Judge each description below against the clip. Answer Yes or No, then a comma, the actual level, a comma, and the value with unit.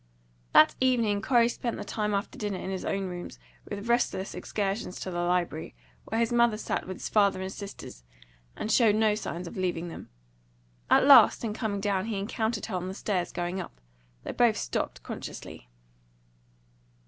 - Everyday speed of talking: Yes, average, 180 wpm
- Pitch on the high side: Yes, high, 200 Hz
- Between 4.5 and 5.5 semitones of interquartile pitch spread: No, average, 3.3 semitones